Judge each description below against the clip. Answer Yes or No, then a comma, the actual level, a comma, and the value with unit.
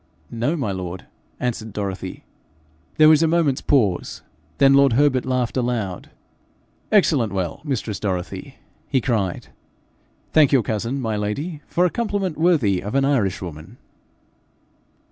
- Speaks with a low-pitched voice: Yes, low, 125 Hz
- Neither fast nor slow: No, slow, 130 wpm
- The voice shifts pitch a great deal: Yes, wide, 6.3 semitones